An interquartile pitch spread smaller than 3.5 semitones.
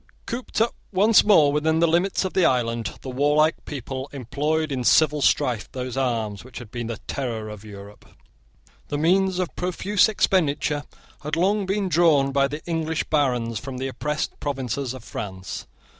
No: average, 4.9 semitones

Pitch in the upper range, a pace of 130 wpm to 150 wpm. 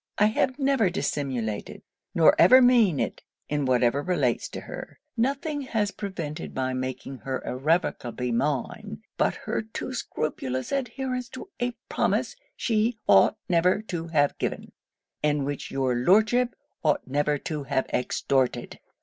No: medium, 160 Hz; average, 140 wpm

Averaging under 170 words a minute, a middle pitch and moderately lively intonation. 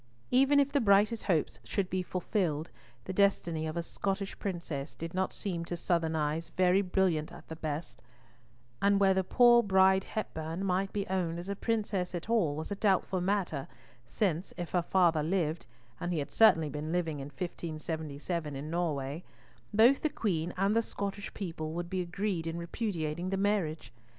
No: average, 175 wpm; medium, 180 Hz; average, 3.6 semitones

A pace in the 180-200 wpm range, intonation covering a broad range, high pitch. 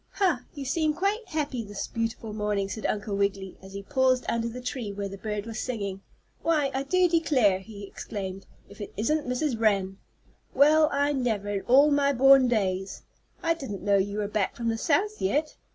Yes: average, 195 wpm; wide, 6.0 semitones; high, 230 Hz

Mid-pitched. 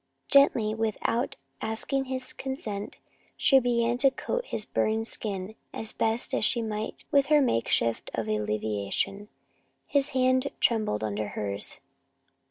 No: high, 220 Hz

